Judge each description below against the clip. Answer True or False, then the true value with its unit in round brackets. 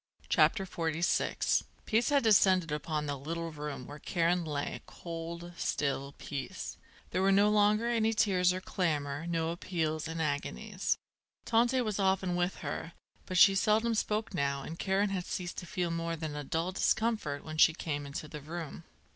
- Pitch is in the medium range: True (170 Hz)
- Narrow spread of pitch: False (4.1 semitones)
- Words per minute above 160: True (170 wpm)